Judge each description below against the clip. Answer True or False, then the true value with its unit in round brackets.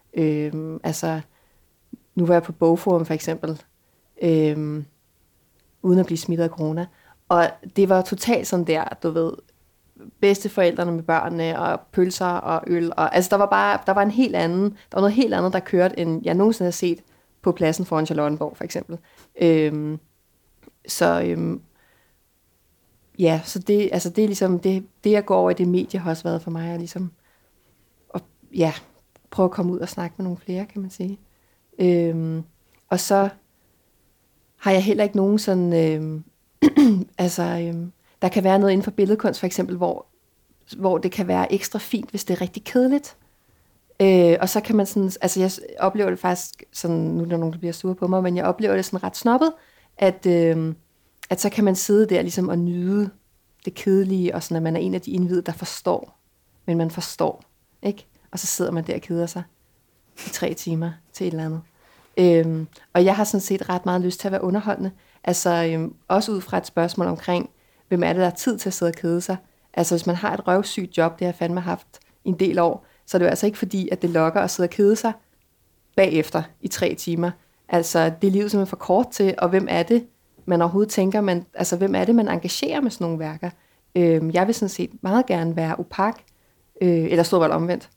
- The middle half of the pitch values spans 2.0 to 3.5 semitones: True (2.8 semitones)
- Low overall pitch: False (180 Hz)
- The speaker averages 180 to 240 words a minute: True (210 wpm)